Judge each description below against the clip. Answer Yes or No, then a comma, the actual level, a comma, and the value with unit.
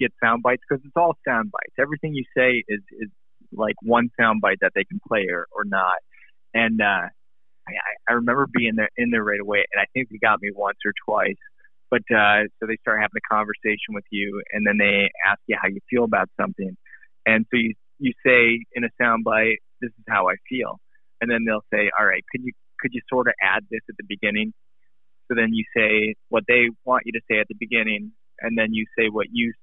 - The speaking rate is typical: No, fast, 230 wpm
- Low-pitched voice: Yes, low, 110 Hz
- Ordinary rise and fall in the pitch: No, narrow, 2.3 semitones